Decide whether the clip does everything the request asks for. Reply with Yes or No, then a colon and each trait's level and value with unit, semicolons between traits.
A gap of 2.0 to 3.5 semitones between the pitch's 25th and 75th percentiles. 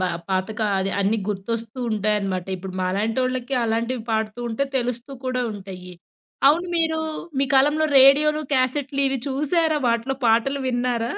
No: average, 4.3 semitones